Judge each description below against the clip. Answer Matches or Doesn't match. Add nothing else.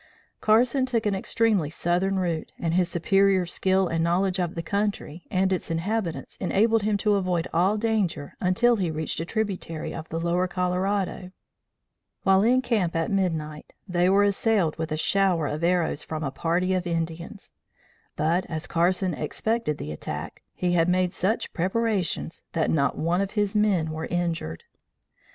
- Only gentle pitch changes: Doesn't match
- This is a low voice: Doesn't match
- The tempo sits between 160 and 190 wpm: Matches